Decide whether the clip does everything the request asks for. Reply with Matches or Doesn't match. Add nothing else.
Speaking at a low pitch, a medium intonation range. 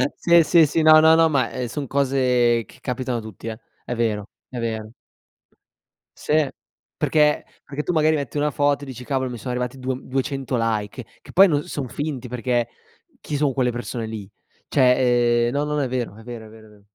Matches